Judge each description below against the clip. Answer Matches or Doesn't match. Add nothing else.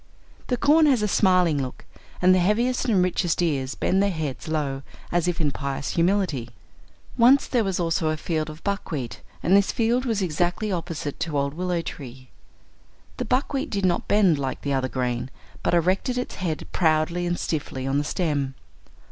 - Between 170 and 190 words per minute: Matches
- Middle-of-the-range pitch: Matches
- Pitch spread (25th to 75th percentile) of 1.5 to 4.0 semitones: Doesn't match